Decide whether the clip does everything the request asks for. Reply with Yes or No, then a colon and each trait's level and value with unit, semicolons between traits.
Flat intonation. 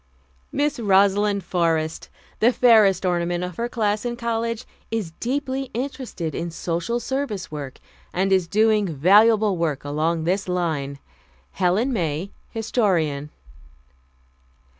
No: average, 5.2 semitones